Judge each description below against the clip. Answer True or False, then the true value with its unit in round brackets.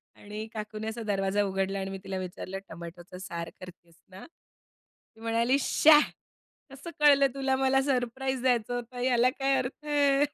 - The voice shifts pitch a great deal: True (5.7 semitones)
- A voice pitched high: True (235 Hz)